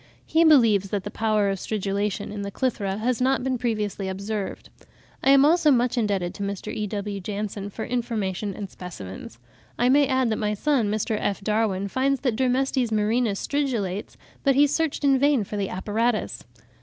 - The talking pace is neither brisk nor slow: Yes, average, 180 wpm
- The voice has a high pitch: Yes, high, 215 Hz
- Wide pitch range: No, average, 4.3 semitones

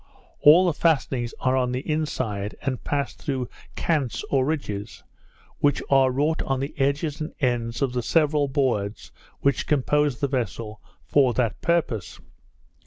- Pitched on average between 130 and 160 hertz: Yes, low, 135 Hz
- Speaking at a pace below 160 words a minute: Yes, average, 150 wpm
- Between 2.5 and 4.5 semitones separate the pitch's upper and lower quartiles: Yes, average, 3.3 semitones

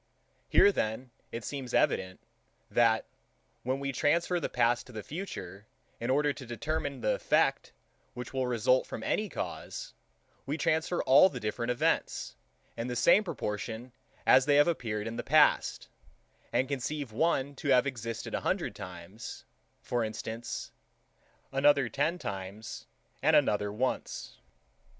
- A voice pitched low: Yes, low, 125 Hz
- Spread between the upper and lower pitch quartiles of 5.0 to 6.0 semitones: No, average, 4.3 semitones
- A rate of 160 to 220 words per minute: No, average, 145 wpm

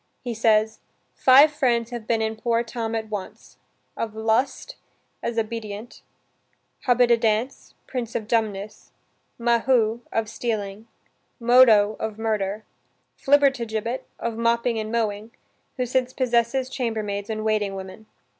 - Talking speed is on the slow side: Yes, slow, 120 wpm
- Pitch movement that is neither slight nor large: No, narrow, 1.8 semitones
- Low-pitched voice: No, high, 225 Hz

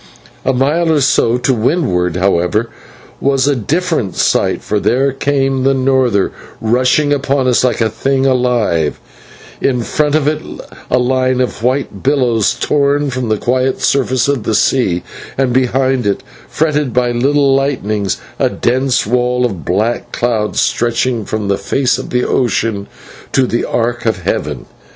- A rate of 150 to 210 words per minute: Yes, average, 155 wpm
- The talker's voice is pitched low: Yes, low, 125 Hz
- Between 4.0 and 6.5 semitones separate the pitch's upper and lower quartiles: No, average, 3.2 semitones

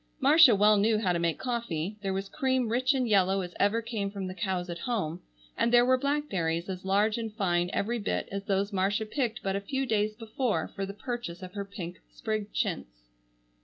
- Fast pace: Yes, fast, 210 wpm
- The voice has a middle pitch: No, high, 205 Hz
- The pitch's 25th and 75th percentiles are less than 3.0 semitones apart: No, average, 3.8 semitones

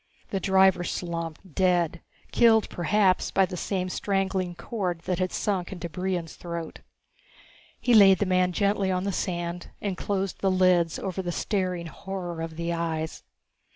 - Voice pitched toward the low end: No, medium, 185 Hz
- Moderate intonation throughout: No, narrow, 2.0 semitones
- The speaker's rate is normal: Yes, average, 155 wpm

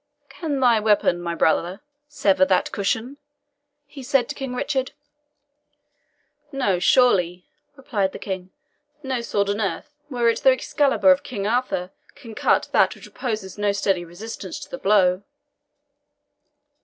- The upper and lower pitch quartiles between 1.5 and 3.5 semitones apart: No, wide, 5.4 semitones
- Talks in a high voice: Yes, high, 215 Hz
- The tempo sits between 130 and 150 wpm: Yes, average, 145 wpm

